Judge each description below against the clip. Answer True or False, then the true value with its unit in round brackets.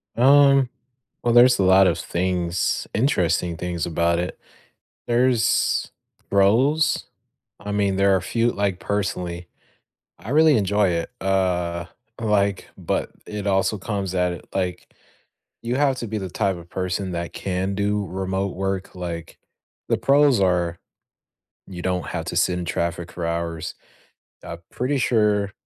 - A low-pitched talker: True (95 Hz)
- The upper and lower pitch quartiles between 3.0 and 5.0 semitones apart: True (3.4 semitones)